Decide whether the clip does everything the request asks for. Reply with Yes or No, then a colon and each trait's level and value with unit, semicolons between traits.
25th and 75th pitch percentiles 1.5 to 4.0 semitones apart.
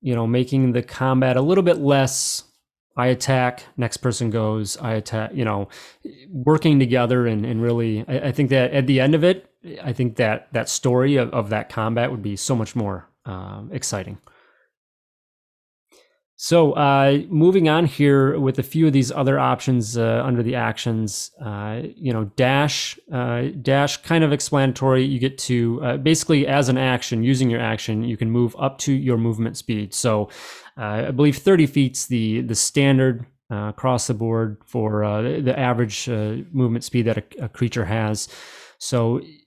Yes: average, 3.1 semitones